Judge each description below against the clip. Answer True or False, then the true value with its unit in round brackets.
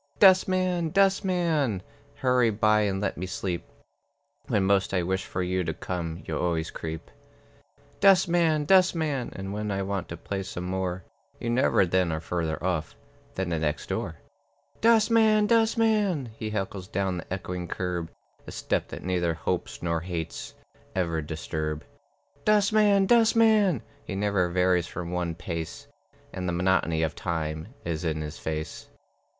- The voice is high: False (95 Hz)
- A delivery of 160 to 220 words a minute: False (150 wpm)